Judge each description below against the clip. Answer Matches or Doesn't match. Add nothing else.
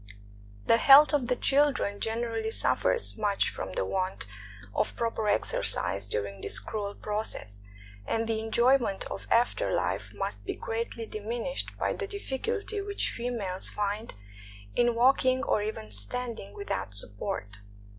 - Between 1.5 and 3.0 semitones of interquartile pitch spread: Doesn't match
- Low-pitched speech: Doesn't match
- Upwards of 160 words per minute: Doesn't match